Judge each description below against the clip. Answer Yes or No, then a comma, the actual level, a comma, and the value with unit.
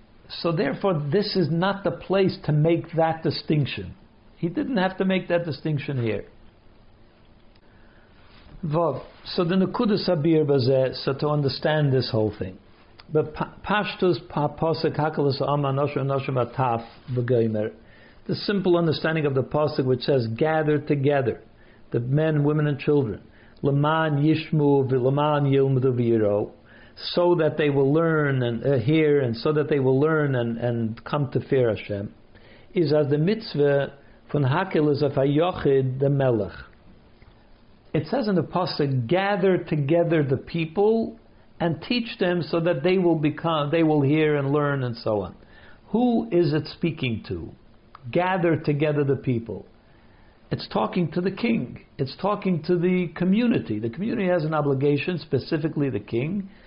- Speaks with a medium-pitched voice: Yes, medium, 145 Hz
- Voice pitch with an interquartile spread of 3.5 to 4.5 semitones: No, average, 5.2 semitones